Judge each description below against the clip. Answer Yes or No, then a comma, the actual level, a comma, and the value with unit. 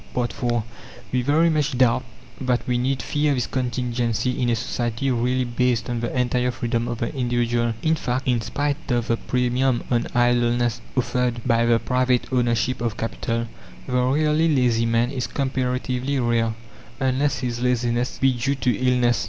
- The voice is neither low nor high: No, low, 125 Hz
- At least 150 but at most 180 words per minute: Yes, average, 165 wpm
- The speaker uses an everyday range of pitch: No, narrow, 1.5 semitones